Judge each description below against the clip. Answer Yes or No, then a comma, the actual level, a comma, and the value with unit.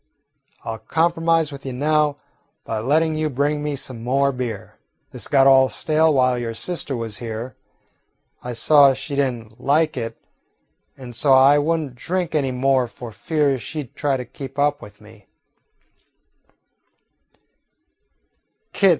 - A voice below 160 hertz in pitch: Yes, low, 135 Hz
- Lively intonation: No, average, 3.5 semitones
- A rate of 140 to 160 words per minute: Yes, average, 150 wpm